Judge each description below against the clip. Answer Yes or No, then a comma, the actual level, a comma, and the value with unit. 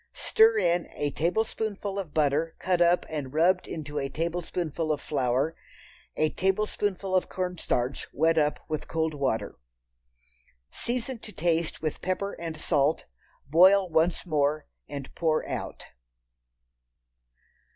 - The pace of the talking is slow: Yes, slow, 125 wpm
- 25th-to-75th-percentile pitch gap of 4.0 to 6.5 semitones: No, average, 3.6 semitones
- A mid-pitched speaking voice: Yes, medium, 165 Hz